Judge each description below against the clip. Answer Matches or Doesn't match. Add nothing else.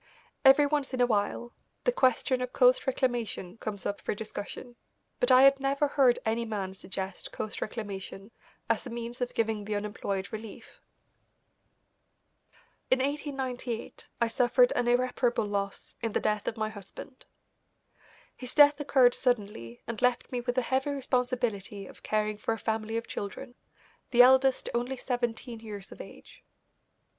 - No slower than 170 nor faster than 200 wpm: Doesn't match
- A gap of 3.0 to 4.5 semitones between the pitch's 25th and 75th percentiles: Matches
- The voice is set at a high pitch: Matches